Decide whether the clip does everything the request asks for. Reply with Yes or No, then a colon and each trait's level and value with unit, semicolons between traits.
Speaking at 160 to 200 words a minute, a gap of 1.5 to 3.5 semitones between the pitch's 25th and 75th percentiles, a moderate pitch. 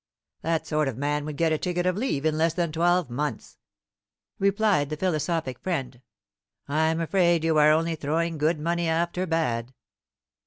Yes: average, 165 wpm; narrow, 2.4 semitones; medium, 160 Hz